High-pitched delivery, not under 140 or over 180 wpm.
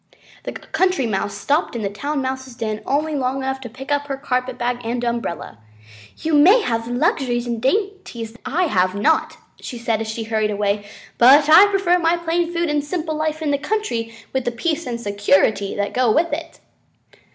No: very high, 260 Hz; average, 195 wpm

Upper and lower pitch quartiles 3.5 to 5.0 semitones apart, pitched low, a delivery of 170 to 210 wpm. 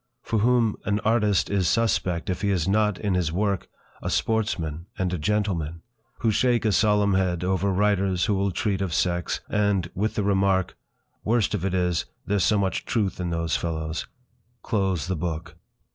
No: average, 3.0 semitones; very low, 95 Hz; average, 180 wpm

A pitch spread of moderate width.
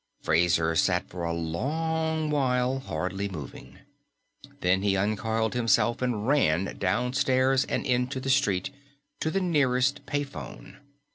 No: wide, 6.4 semitones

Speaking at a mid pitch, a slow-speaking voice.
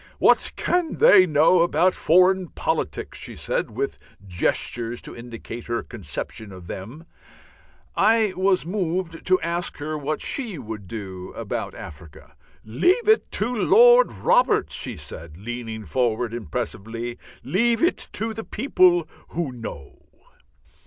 Yes: medium, 155 Hz; slow, 130 wpm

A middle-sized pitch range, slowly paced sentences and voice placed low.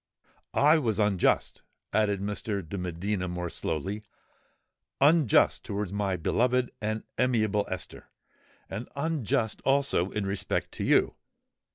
Yes: average, 4.0 semitones; slow, 105 wpm; low, 105 Hz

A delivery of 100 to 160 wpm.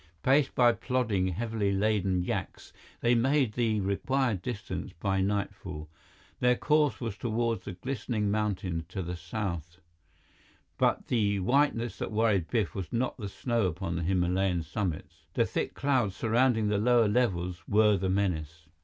Yes: average, 150 wpm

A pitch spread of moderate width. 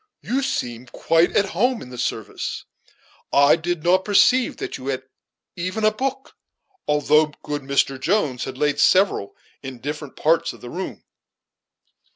No: wide, 6.6 semitones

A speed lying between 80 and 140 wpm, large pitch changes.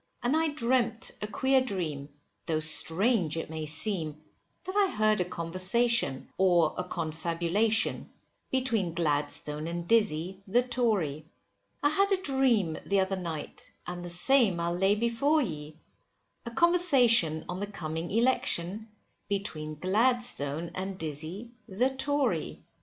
Yes: slow, 135 wpm; wide, 6.6 semitones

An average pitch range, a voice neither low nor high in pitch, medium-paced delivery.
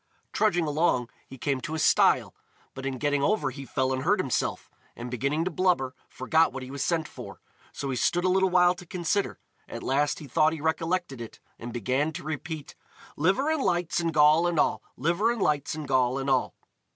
No: average, 4.6 semitones; medium, 155 Hz; fast, 210 wpm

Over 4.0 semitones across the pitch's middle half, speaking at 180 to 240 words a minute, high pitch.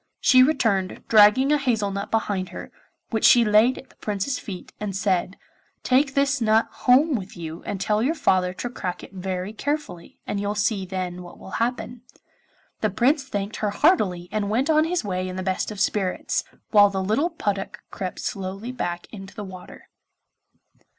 Yes: average, 4.8 semitones; average, 185 wpm; high, 205 Hz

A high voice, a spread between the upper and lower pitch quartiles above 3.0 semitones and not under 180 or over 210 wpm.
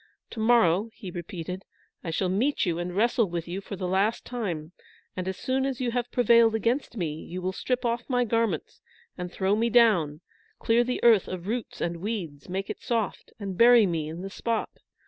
Yes: high, 200 Hz; average, 4.7 semitones; fast, 205 wpm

